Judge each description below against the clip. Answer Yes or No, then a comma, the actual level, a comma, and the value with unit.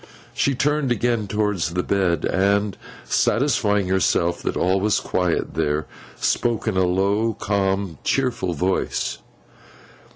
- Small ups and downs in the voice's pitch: No, average, 3.5 semitones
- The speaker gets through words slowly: Yes, slow, 125 wpm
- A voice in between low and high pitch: No, low, 100 Hz